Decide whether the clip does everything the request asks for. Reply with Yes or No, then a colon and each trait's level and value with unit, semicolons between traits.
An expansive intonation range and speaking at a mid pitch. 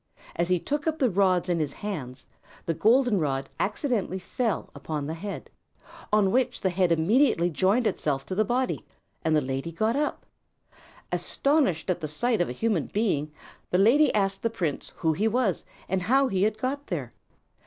No: wide, 6.3 semitones; high, 195 Hz